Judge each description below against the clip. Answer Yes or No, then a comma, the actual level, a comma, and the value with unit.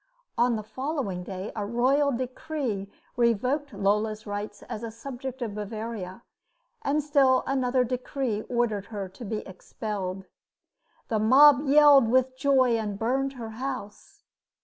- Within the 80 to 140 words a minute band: Yes, slow, 135 wpm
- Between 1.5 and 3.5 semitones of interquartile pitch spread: No, average, 4.2 semitones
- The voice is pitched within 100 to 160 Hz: No, high, 235 Hz